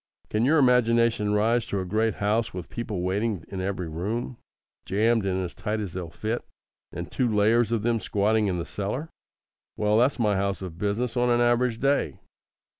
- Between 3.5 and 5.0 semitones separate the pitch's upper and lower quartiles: No, average, 3.1 semitones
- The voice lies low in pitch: Yes, low, 110 Hz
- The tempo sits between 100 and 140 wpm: No, average, 190 wpm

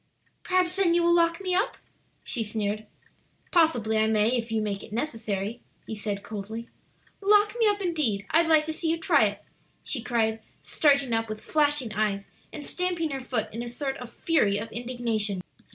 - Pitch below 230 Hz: No, high, 240 Hz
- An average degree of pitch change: No, wide, 7.0 semitones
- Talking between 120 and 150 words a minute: No, average, 185 wpm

